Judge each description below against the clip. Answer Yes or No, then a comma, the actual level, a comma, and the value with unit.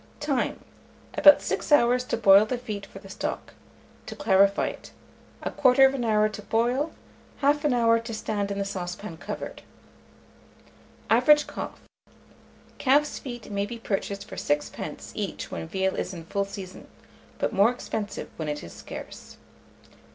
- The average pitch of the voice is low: No, high, 215 Hz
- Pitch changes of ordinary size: Yes, average, 4.1 semitones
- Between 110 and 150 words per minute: Yes, average, 145 wpm